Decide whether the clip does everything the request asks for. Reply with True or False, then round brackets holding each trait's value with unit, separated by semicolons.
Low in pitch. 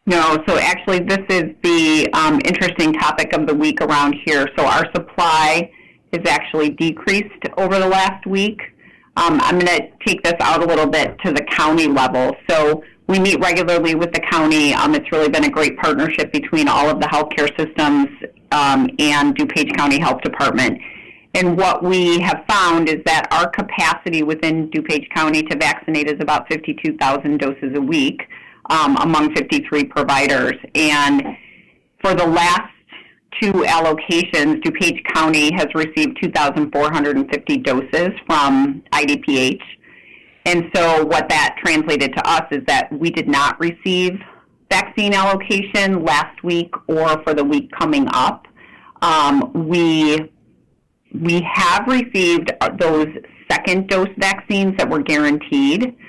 False (165 Hz)